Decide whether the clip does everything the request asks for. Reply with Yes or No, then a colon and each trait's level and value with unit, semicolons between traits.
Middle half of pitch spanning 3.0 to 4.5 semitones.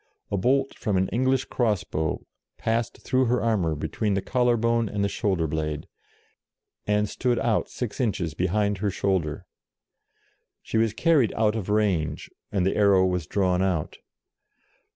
Yes: average, 4.0 semitones